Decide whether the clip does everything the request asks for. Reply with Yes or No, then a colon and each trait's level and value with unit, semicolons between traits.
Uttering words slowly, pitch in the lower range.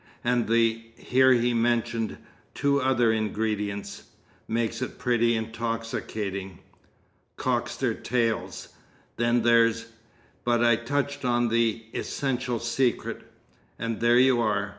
Yes: slow, 115 wpm; low, 115 Hz